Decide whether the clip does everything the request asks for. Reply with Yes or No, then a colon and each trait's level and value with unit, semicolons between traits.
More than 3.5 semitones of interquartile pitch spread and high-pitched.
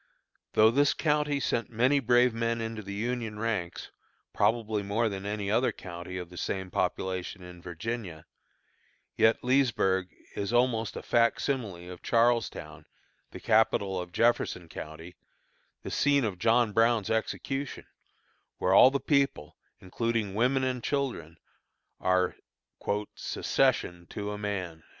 No: average, 4.7 semitones; low, 110 Hz